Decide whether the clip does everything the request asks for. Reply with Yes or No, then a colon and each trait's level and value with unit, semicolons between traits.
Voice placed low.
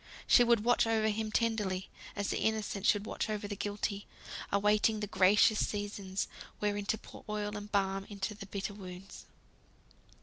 No: high, 205 Hz